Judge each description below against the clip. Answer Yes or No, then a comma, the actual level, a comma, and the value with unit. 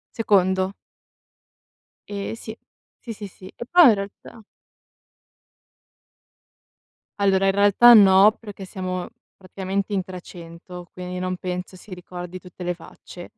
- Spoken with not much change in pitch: Yes, narrow, 2.0 semitones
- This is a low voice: No, high, 190 Hz